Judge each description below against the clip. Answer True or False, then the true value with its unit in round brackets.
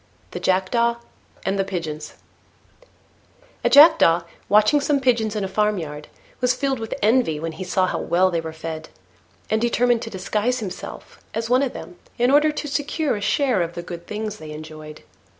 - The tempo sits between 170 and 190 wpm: True (180 wpm)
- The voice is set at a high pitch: True (210 Hz)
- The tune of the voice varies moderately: False (6.3 semitones)